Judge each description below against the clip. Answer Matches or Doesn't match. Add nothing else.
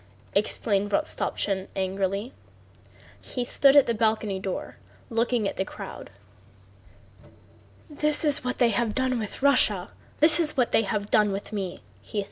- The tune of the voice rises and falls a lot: Doesn't match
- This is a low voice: Doesn't match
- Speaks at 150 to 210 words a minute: Doesn't match